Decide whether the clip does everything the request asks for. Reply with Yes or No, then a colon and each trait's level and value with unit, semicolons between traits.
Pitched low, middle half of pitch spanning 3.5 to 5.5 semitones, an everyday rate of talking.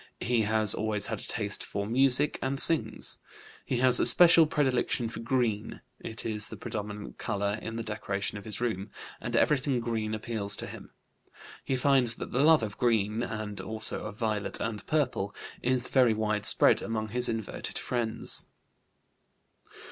No: low, 115 Hz; average, 2.8 semitones; average, 165 wpm